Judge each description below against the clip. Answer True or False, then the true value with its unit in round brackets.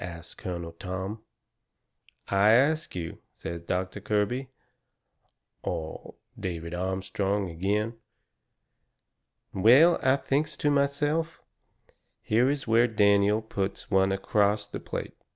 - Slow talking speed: True (105 wpm)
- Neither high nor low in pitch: False (105 Hz)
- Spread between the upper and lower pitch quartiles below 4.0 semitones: False (5.0 semitones)